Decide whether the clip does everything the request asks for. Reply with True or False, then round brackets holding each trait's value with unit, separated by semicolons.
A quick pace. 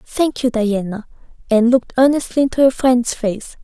False (165 wpm)